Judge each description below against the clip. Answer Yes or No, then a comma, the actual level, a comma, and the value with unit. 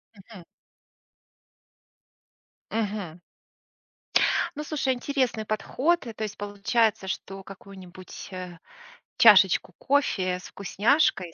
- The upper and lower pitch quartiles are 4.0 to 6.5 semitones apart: Yes, average, 4.3 semitones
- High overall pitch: Yes, high, 205 Hz